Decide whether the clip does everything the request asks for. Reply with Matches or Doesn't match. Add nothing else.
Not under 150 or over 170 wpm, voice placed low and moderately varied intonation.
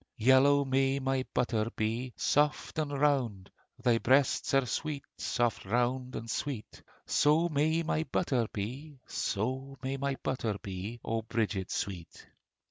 Doesn't match